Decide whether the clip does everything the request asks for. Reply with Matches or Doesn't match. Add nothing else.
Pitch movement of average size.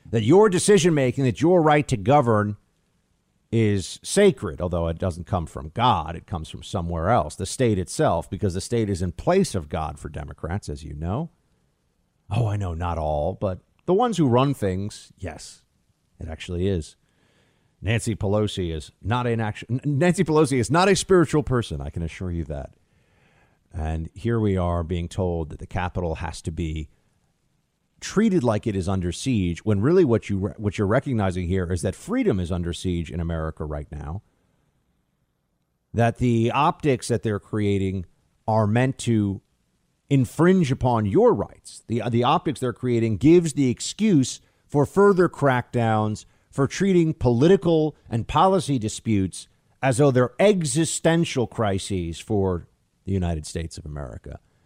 Doesn't match